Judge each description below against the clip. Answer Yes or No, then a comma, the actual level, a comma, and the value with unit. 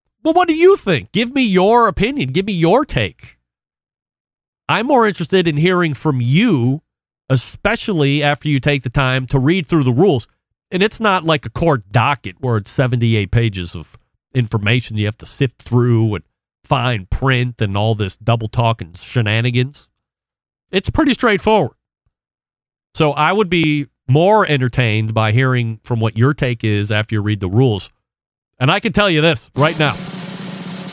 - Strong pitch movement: Yes, wide, 7.7 semitones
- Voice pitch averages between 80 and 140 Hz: Yes, low, 135 Hz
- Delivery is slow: No, average, 175 wpm